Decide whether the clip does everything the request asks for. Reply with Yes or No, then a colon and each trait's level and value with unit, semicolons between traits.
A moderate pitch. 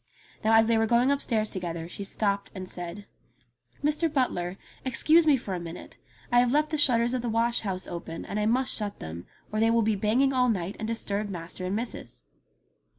No: high, 220 Hz